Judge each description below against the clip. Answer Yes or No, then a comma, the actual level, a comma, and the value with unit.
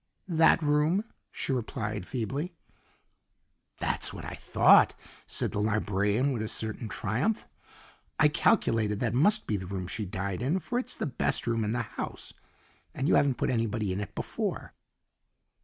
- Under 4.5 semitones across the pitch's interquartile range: No, wide, 5.4 semitones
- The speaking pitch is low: Yes, low, 115 Hz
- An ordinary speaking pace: Yes, average, 160 wpm